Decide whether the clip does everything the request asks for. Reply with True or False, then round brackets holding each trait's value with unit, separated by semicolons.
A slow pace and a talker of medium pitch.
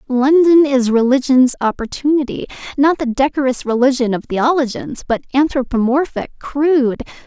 False (100 wpm; 265 Hz)